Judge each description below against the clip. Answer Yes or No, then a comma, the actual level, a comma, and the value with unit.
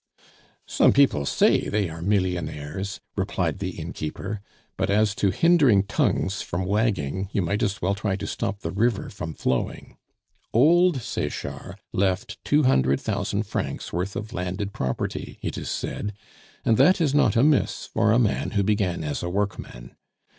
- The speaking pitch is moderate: No, low, 100 Hz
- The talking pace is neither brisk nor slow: Yes, average, 160 wpm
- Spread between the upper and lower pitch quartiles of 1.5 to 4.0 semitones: Yes, average, 3.6 semitones